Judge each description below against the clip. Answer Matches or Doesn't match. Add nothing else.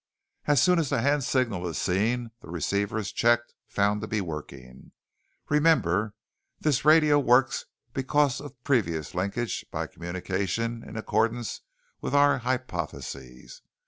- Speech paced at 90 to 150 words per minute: Matches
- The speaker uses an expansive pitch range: Matches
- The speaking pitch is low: Matches